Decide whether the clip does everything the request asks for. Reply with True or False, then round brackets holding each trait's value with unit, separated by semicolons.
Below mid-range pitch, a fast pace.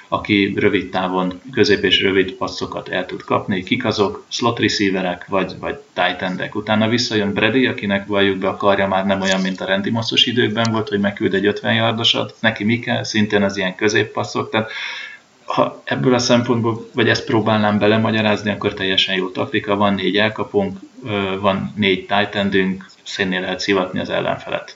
True (100 Hz; 175 wpm)